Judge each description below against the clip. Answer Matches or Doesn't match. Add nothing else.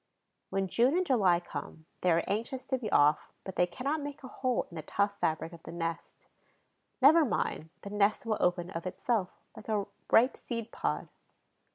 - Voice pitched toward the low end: Doesn't match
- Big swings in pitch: Matches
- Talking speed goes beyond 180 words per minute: Matches